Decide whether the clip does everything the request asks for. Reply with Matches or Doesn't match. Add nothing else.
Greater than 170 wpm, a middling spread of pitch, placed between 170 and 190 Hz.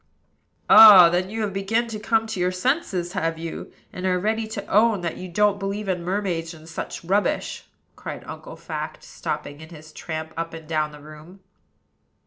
Matches